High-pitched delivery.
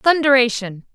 Yes: very high, 250 Hz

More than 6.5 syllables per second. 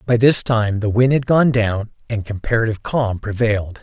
No: 5.1 syllables/s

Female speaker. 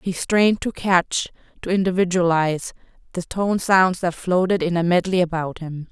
Yes: female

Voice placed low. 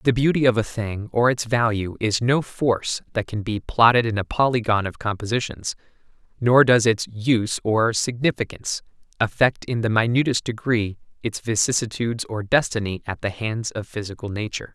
Yes: low, 115 Hz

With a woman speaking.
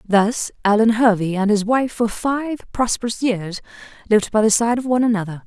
Yes: female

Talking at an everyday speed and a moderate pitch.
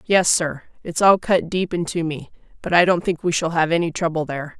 No: fast, 235 wpm; medium, 165 Hz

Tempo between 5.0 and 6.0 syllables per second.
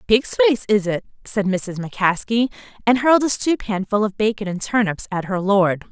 Yes: 5.2 syllables/s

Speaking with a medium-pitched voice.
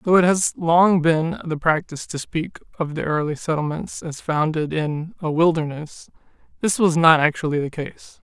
Yes: medium, 160 Hz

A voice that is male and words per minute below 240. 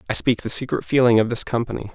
No: male; fast, 245 wpm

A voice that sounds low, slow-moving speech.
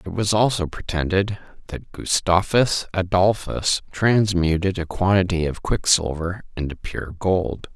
Yes: very low, 90 Hz; slow, 115 wpm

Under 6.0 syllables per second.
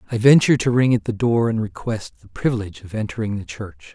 No: 6.4 syllables/s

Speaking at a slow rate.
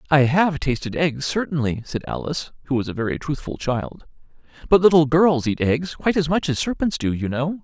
No: fast, 205 wpm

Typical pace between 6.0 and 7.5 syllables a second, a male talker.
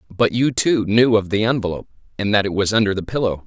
Yes: 6.4 syllables/s; male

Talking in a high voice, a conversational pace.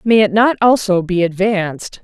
Yes: high, 200 Hz; average, 175 wpm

